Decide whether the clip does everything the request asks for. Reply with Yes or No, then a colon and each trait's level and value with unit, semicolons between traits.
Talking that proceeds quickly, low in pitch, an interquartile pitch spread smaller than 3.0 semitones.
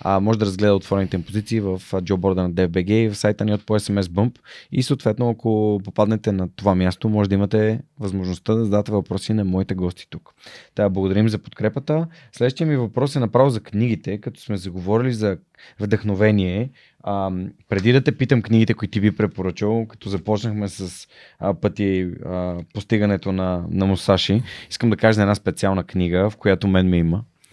Yes: fast, 180 wpm; low, 105 Hz; narrow, 2.6 semitones